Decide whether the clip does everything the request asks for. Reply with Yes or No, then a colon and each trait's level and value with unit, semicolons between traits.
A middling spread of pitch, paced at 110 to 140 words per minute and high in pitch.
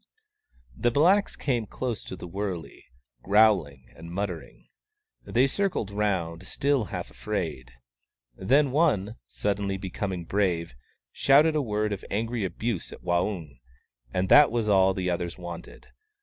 No: average, 5.0 semitones; slow, 135 wpm; low, 100 Hz